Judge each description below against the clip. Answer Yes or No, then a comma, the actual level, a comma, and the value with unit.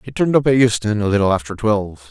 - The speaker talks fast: Yes, fast, 255 wpm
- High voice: No, low, 110 Hz